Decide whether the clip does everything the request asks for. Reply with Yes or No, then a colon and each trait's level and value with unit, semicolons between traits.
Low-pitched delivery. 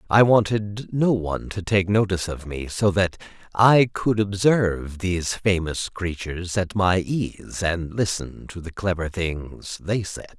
Yes: very low, 95 Hz